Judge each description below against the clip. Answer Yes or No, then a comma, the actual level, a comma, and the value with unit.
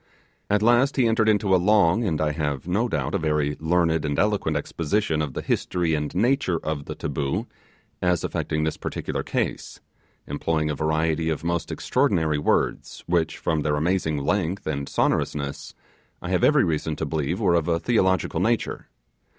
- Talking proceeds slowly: No, average, 175 wpm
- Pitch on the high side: No, very low, 80 Hz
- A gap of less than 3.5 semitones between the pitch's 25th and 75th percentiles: No, average, 3.9 semitones